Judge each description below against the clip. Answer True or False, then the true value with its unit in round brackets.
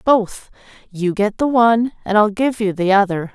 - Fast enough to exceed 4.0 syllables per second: True (4.7 syllables/s)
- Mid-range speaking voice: False (210 Hz)